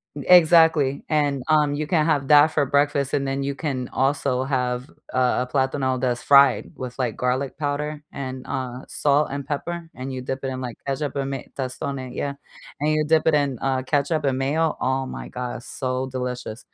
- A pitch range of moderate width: No, narrow, 2.2 semitones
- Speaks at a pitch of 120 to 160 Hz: Yes, low, 135 Hz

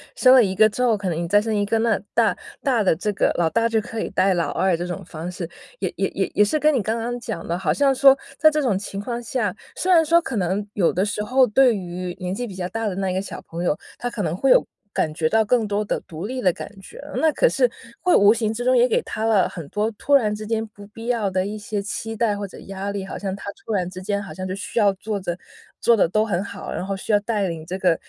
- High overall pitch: Yes, high, 205 Hz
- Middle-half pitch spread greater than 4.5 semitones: No, average, 3.6 semitones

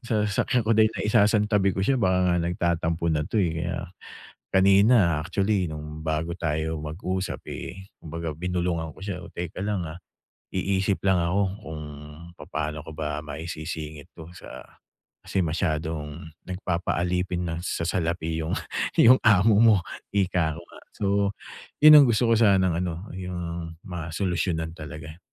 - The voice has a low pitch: Yes, very low, 85 Hz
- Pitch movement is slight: No, average, 3.2 semitones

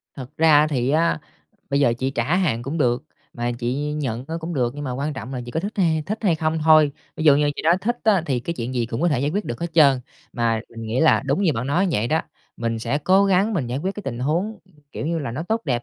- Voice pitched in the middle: Yes, medium, 145 Hz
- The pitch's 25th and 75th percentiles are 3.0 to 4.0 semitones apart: No, average, 5.1 semitones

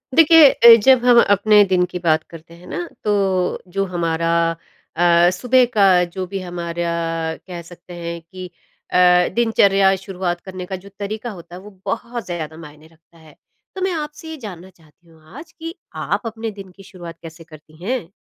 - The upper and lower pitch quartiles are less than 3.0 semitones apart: No, average, 3.7 semitones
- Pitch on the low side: No, medium, 180 Hz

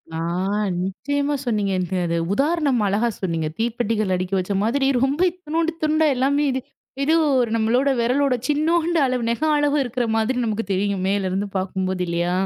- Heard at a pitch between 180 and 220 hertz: No, high, 235 Hz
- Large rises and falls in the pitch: Yes, wide, 6.6 semitones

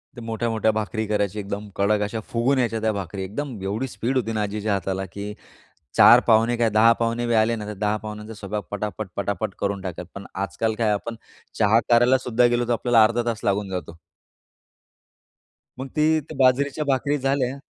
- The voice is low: Yes, low, 110 Hz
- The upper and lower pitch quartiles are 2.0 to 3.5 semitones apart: Yes, average, 2.8 semitones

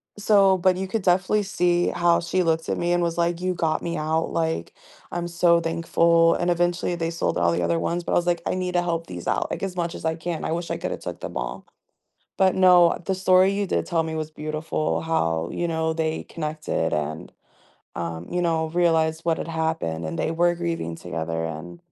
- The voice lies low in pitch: No, medium, 165 Hz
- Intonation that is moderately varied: No, narrow, 1.9 semitones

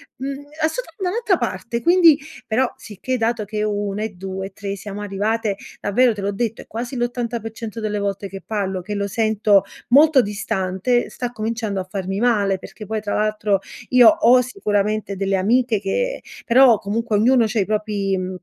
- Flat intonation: No, average, 3.3 semitones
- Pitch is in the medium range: No, high, 215 Hz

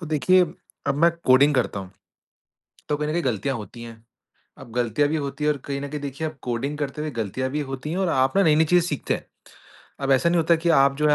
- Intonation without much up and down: No, average, 3.0 semitones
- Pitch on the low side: No, medium, 145 Hz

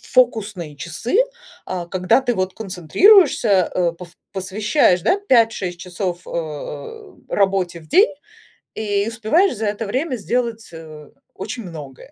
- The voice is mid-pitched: No, high, 200 Hz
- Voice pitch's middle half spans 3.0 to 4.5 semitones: No, average, 5.1 semitones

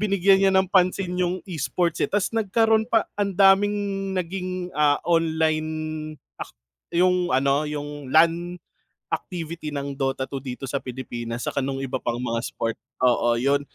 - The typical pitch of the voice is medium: Yes, medium, 165 Hz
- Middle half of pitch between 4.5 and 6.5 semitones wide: Yes, average, 5.1 semitones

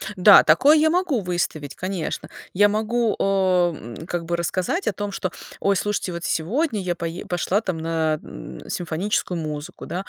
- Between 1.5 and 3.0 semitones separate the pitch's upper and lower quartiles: No, average, 3.8 semitones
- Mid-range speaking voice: Yes, medium, 180 Hz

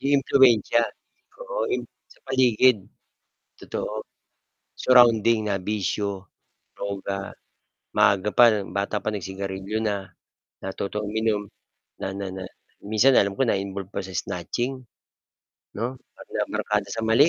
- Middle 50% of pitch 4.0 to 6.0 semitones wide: No, average, 3.2 semitones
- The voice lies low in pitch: Yes, low, 105 Hz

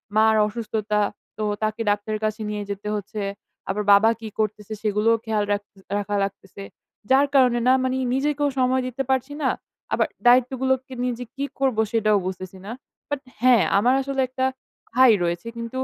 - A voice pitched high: Yes, high, 225 Hz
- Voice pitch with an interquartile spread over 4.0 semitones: No, average, 3.7 semitones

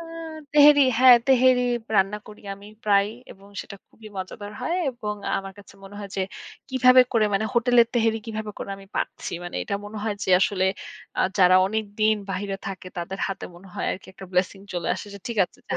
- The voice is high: Yes, high, 205 Hz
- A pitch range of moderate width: Yes, average, 3.1 semitones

